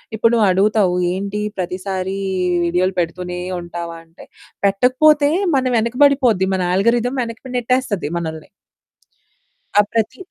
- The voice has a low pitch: No, high, 200 Hz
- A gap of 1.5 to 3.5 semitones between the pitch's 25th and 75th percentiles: No, average, 4.7 semitones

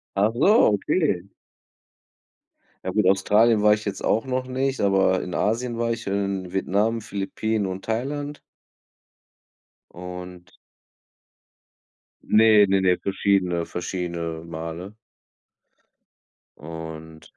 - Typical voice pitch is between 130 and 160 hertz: No, low, 100 Hz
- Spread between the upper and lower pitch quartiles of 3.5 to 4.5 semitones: Yes, average, 3.8 semitones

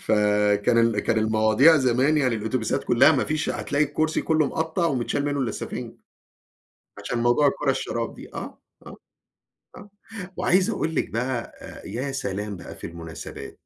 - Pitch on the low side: Yes, low, 125 Hz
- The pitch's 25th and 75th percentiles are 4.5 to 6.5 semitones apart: Yes, average, 5.2 semitones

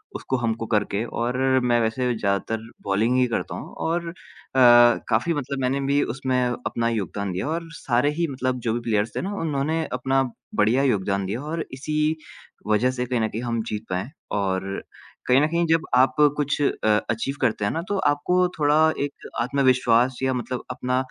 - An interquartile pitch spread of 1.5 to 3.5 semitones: No, average, 4.0 semitones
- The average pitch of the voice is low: Yes, low, 125 Hz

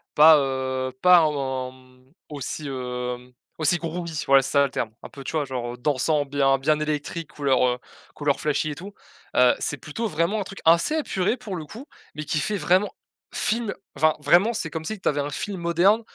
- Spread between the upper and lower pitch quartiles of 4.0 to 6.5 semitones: Yes, average, 4.4 semitones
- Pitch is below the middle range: No, medium, 150 Hz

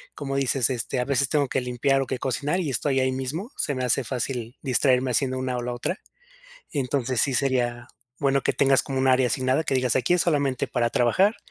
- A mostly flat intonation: Yes, narrow, 1.9 semitones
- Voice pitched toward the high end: No, low, 130 Hz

